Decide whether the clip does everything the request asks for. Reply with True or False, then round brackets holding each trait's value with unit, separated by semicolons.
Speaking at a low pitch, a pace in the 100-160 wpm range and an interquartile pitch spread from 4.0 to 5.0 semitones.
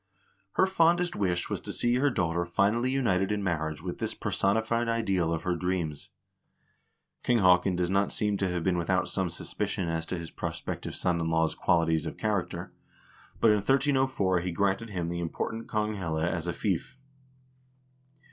False (95 Hz; 170 wpm; 4.3 semitones)